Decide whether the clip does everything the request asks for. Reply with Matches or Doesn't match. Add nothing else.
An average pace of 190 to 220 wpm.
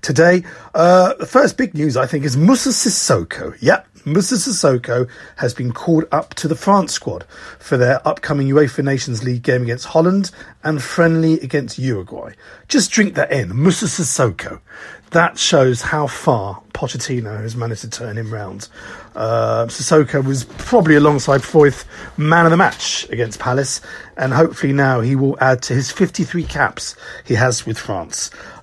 Doesn't match